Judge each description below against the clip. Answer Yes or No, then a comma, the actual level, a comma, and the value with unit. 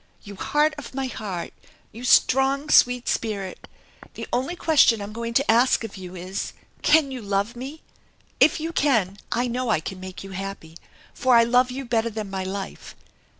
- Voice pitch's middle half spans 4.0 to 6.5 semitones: Yes, average, 4.9 semitones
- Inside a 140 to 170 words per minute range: No, average, 185 wpm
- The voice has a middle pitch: No, high, 230 Hz